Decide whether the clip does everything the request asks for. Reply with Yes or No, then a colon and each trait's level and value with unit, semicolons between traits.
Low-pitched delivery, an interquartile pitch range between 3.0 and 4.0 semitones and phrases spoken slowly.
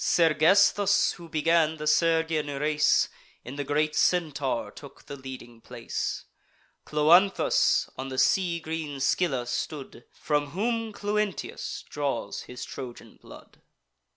No: medium, 155 Hz; average, 3.3 semitones; slow, 120 wpm